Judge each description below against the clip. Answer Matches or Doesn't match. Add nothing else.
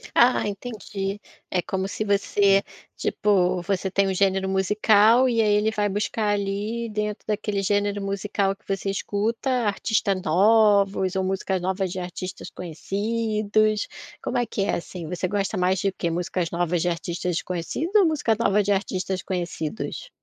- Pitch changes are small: Matches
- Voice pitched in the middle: Doesn't match